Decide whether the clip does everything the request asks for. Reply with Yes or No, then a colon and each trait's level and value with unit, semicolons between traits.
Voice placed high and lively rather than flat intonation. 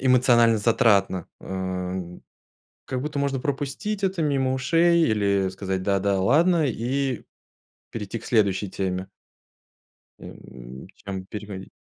No: low, 110 Hz; wide, 6.2 semitones